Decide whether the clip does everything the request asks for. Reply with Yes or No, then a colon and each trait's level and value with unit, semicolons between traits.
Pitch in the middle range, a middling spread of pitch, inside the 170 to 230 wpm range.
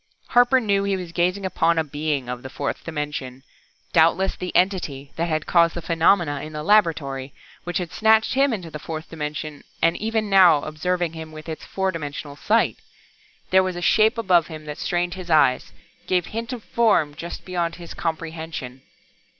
Yes: medium, 170 Hz; average, 3.6 semitones; average, 185 wpm